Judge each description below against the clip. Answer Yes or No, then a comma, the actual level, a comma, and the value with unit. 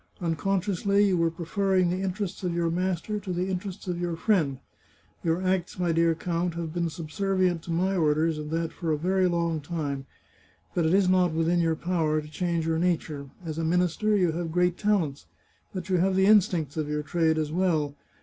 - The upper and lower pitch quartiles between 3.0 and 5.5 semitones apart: No, narrow, 2.4 semitones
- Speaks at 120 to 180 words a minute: No, fast, 205 wpm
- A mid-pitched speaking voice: Yes, medium, 170 Hz